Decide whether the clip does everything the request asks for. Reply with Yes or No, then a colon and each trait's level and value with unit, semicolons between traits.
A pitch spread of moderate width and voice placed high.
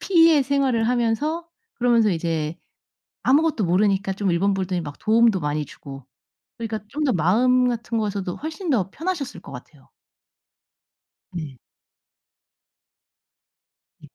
No: wide, 6.6 semitones; high, 220 Hz